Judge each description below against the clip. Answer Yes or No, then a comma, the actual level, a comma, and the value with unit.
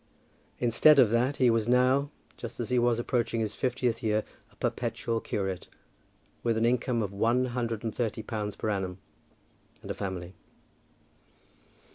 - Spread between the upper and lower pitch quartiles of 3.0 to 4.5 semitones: No, narrow, 2.5 semitones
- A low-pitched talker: Yes, low, 115 Hz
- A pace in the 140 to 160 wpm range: Yes, average, 155 wpm